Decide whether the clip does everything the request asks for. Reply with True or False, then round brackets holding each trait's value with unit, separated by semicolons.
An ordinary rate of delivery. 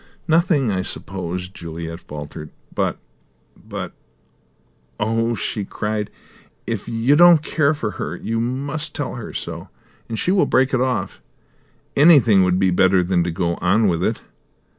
True (150 wpm)